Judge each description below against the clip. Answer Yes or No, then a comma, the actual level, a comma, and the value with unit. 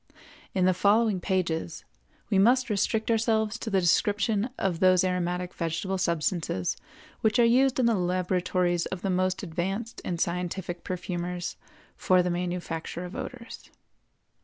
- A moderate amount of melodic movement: Yes, average, 3.0 semitones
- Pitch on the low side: No, medium, 185 Hz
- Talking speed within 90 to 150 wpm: Yes, average, 140 wpm